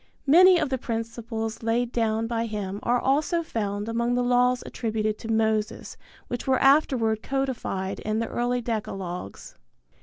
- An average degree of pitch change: No, narrow, 2.3 semitones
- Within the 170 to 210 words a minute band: No, average, 150 wpm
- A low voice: No, high, 230 Hz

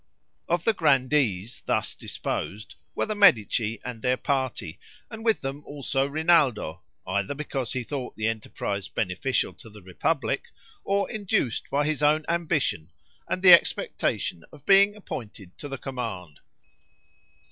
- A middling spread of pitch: No, wide, 6.5 semitones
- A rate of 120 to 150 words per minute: Yes, average, 140 wpm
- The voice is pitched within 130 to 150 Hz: Yes, low, 135 Hz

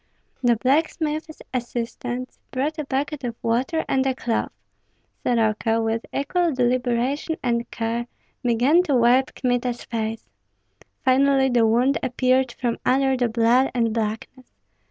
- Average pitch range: No, narrow, 2.3 semitones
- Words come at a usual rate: No, slow, 130 wpm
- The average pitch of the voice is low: No, very high, 250 Hz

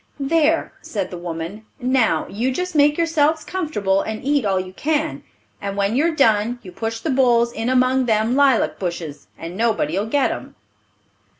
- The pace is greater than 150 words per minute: Yes, average, 170 wpm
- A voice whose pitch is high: Yes, high, 235 Hz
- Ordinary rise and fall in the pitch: No, wide, 6.3 semitones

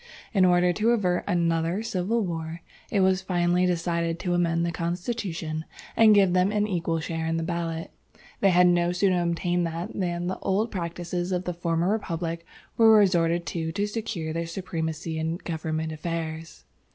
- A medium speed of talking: Yes, average, 170 wpm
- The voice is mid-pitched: Yes, medium, 175 Hz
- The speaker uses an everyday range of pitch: No, narrow, 2.0 semitones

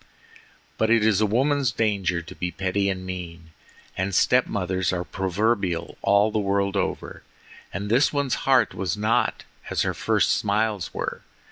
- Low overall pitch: Yes, low, 100 Hz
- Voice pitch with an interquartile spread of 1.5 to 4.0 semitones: Yes, average, 3.0 semitones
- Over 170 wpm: No, average, 160 wpm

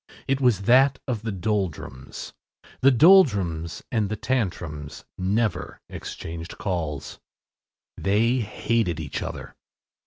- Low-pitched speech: Yes, low, 105 Hz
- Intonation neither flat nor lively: No, wide, 5.9 semitones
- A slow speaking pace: Yes, slow, 105 wpm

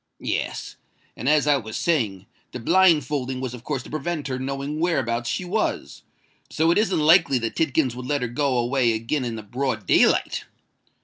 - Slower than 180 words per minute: No, average, 190 wpm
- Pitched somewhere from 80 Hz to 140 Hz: Yes, low, 135 Hz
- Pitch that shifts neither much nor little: Yes, average, 4.2 semitones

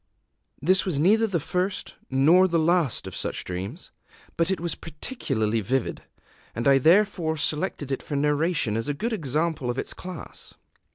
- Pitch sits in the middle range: Yes, medium, 160 Hz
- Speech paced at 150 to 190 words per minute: Yes, average, 165 wpm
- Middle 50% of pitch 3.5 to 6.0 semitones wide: Yes, average, 5.2 semitones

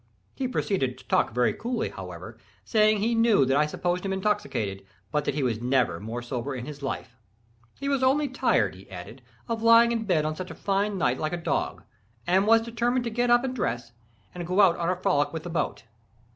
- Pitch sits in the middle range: Yes, medium, 180 Hz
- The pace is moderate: No, fast, 220 wpm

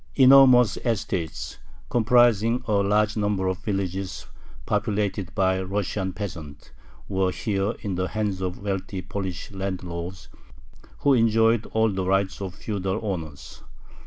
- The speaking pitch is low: Yes, low, 100 Hz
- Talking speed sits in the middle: No, slow, 125 wpm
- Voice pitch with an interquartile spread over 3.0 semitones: No, narrow, 2.6 semitones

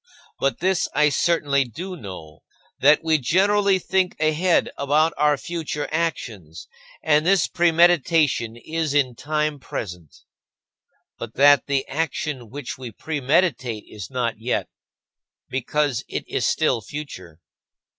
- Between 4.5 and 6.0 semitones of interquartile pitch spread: Yes, average, 4.8 semitones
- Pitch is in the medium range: Yes, medium, 145 Hz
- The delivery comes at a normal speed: No, slow, 125 wpm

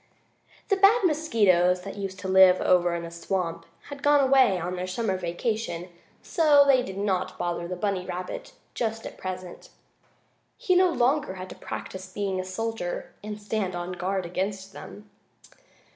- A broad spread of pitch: No, average, 4.1 semitones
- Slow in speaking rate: No, average, 170 wpm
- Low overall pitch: No, high, 190 Hz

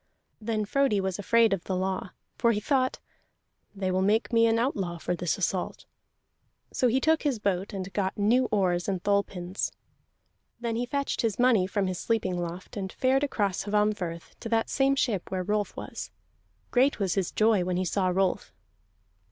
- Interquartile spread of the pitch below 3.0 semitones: No, average, 3.8 semitones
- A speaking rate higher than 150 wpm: Yes, average, 185 wpm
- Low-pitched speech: No, high, 205 Hz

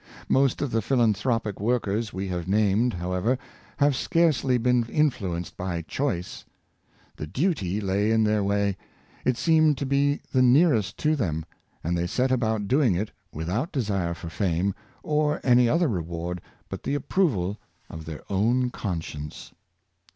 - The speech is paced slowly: No, average, 155 wpm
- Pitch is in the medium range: No, low, 110 Hz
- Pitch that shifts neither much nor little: No, wide, 6.3 semitones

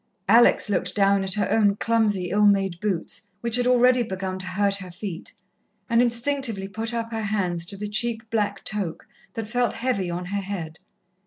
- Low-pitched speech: No, high, 205 Hz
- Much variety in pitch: No, average, 3.2 semitones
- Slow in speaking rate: No, average, 185 wpm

